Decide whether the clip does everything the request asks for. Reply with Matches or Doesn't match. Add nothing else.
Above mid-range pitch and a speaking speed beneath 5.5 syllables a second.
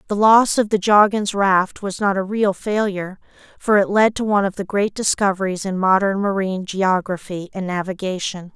Matches